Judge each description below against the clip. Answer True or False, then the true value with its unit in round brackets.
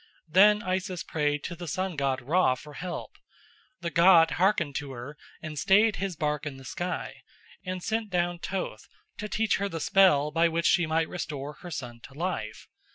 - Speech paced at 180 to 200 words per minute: True (185 wpm)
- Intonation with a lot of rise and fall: False (4.1 semitones)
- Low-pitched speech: False (170 Hz)